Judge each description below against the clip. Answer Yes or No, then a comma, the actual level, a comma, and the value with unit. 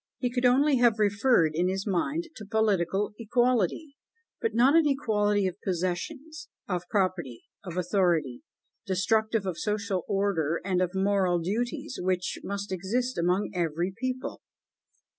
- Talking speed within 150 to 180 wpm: No, average, 140 wpm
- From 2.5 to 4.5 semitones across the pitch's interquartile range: No, average, 5.1 semitones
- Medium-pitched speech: No, high, 200 Hz